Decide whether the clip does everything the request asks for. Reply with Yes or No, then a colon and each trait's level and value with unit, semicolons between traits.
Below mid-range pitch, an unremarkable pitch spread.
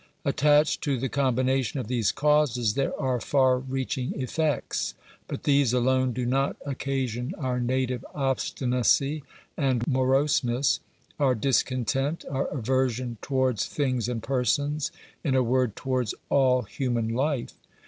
No: low, 130 Hz; narrow, 1.8 semitones